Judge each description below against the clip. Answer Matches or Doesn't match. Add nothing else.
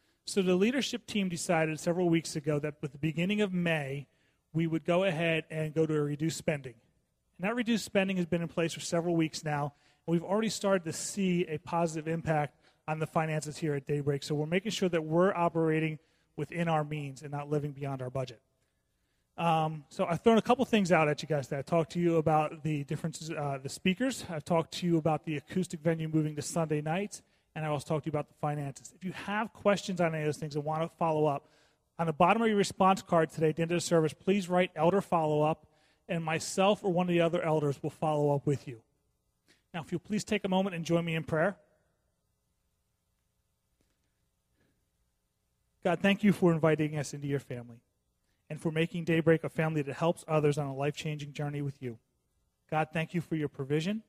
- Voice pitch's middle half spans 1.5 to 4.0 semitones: Matches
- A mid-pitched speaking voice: Matches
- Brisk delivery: Matches